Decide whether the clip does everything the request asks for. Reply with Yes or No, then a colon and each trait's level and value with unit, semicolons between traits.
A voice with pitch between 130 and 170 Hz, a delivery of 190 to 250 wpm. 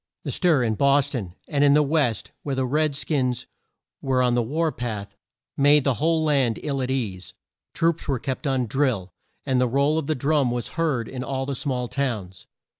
Yes: low, 135 Hz; average, 200 wpm